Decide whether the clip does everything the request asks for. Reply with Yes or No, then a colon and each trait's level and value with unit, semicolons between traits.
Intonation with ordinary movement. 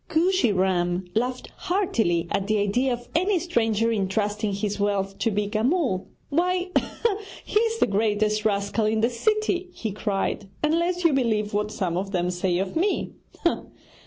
No: wide, 8.1 semitones